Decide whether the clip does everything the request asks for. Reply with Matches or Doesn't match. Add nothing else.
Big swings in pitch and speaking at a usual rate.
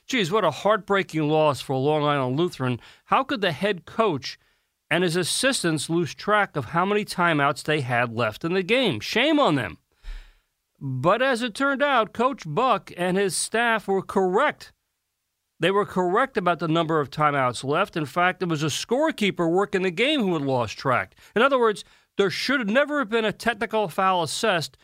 Matches